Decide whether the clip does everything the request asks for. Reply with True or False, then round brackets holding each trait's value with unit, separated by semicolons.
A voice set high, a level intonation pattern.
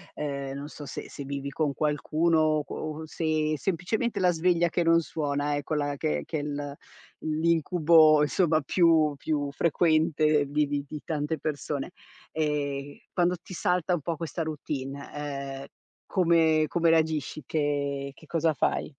False (155 Hz; 2.3 semitones)